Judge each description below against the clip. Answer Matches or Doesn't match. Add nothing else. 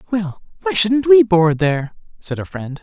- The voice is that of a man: Matches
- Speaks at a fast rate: Doesn't match